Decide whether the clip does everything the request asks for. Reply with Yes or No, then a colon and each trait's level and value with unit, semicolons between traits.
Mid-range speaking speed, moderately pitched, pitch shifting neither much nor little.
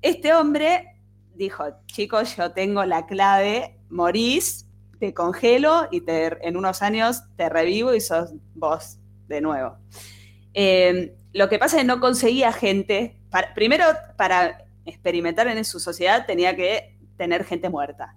No: average, 145 wpm; medium, 180 Hz; wide, 6.9 semitones